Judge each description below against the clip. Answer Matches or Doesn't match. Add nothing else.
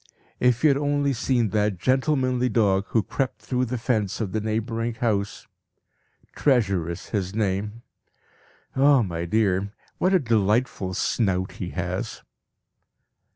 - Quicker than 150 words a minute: Doesn't match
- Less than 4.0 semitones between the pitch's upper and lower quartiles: Doesn't match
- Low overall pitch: Matches